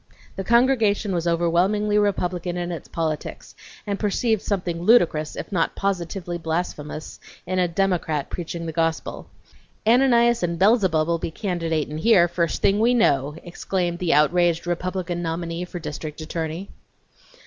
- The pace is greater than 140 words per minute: No, slow, 135 wpm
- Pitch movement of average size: Yes, average, 3.2 semitones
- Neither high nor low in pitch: Yes, medium, 175 Hz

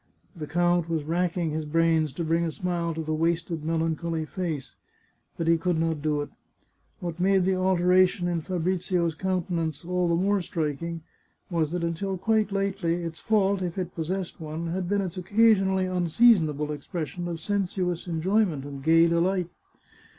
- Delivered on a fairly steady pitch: Yes, narrow, 2.3 semitones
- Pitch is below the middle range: No, medium, 170 Hz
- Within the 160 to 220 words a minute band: Yes, average, 170 wpm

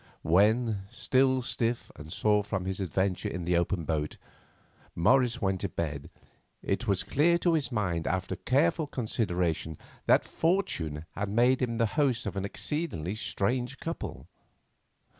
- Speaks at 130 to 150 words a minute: Yes, average, 145 wpm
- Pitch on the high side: No, low, 105 Hz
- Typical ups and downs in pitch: No, wide, 6.2 semitones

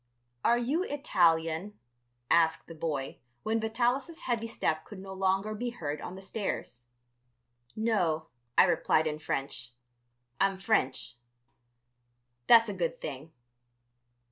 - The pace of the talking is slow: Yes, slow, 120 wpm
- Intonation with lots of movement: Yes, wide, 6.0 semitones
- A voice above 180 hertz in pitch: Yes, high, 190 Hz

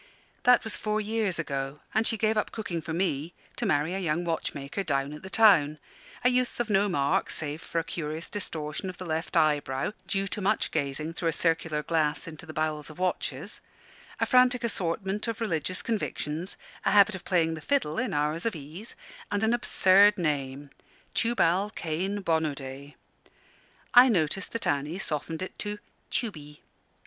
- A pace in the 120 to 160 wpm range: No, average, 175 wpm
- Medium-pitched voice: Yes, medium, 170 Hz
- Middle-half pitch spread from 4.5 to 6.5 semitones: Yes, average, 5.3 semitones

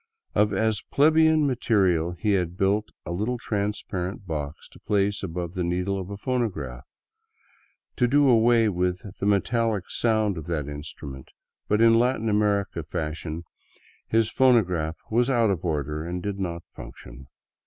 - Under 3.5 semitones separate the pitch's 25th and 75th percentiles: No, average, 4.8 semitones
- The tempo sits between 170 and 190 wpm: No, average, 155 wpm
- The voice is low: Yes, low, 100 Hz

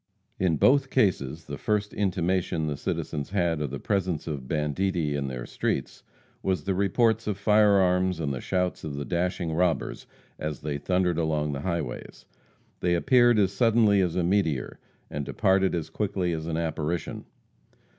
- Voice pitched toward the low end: Yes, very low, 90 Hz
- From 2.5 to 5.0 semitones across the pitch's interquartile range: Yes, average, 4.2 semitones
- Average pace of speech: Yes, average, 165 wpm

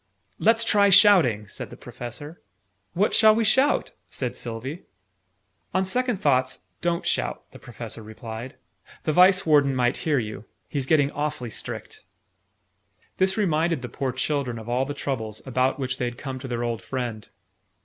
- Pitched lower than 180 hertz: Yes, low, 135 Hz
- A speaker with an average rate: Yes, average, 160 wpm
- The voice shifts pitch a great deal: Yes, wide, 6.3 semitones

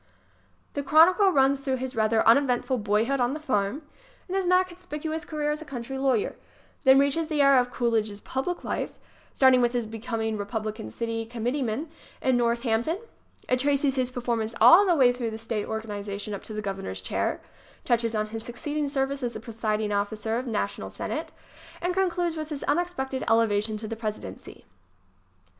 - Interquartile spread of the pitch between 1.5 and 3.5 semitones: No, average, 4.5 semitones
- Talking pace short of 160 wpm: No, average, 185 wpm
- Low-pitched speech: No, high, 245 Hz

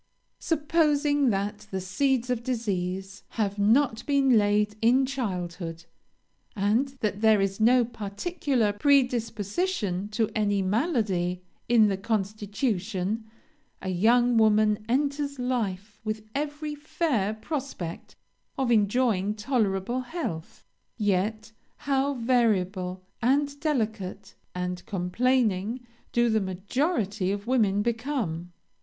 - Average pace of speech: No, slow, 105 wpm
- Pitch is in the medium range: No, high, 220 Hz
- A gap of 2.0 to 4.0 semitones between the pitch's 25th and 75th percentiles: No, average, 4.6 semitones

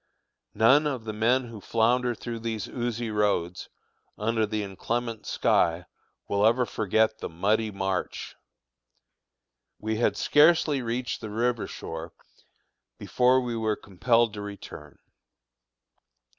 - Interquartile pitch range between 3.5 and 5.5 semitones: No, average, 2.8 semitones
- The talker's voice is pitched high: No, low, 110 Hz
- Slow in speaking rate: Yes, slow, 120 wpm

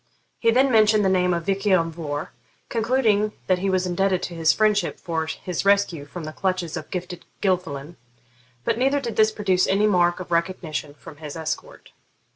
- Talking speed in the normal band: Yes, average, 185 wpm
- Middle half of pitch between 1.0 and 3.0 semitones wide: No, average, 3.9 semitones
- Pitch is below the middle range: No, medium, 185 Hz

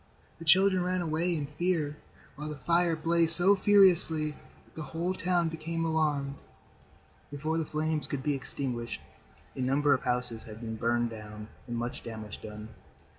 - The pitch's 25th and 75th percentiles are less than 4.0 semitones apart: No, average, 5.2 semitones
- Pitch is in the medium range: Yes, medium, 150 Hz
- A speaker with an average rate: Yes, average, 165 wpm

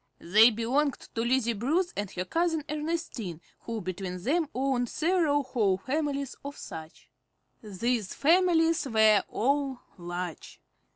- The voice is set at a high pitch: Yes, very high, 250 Hz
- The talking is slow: Yes, slow, 125 wpm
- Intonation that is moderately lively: No, wide, 6.5 semitones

